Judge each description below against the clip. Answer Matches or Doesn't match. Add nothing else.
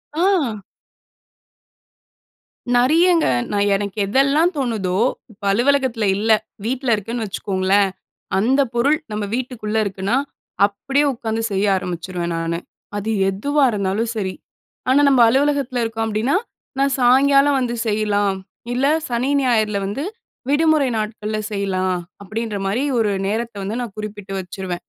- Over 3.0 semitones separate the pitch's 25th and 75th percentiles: Matches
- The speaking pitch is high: Matches